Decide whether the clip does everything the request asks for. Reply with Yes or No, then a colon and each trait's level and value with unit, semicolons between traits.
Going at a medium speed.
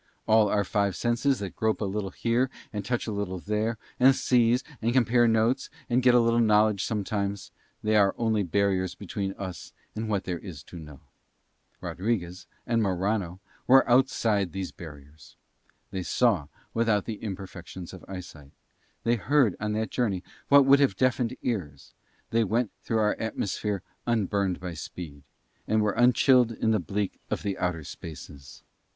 Yes: average, 165 wpm